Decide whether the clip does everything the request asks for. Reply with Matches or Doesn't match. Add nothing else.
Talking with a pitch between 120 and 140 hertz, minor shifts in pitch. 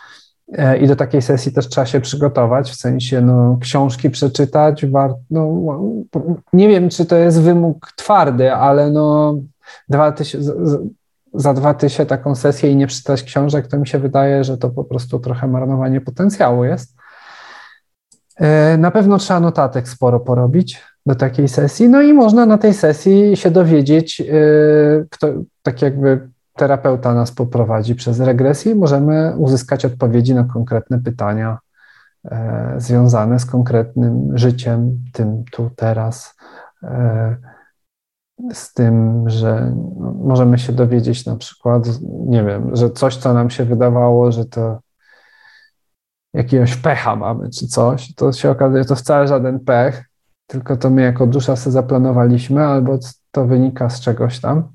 Doesn't match